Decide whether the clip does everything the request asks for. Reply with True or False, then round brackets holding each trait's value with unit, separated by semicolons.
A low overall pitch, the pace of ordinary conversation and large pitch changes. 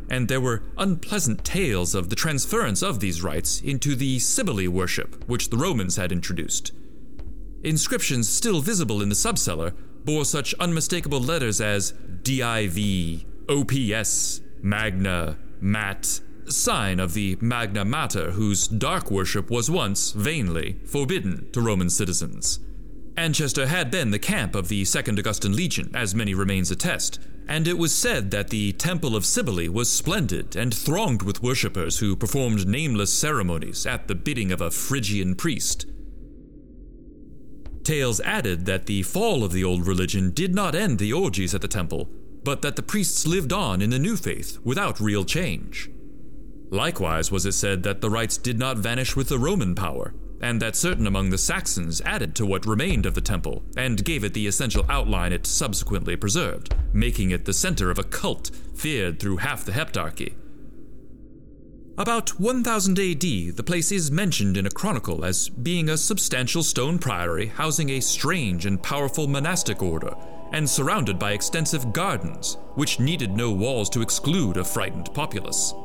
True (110 Hz; 160 wpm; 6.8 semitones)